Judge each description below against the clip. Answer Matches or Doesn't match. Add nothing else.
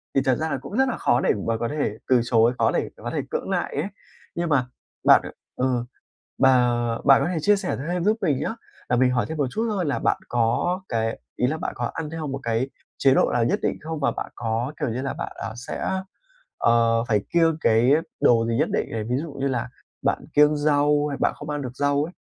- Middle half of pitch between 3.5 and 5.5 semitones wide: Matches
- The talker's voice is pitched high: Doesn't match